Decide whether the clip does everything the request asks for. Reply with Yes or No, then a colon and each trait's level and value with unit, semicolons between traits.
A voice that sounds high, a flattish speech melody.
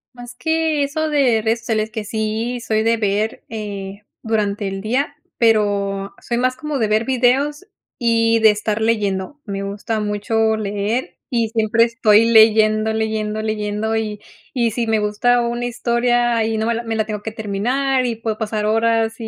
Yes: high, 220 Hz; narrow, 2.0 semitones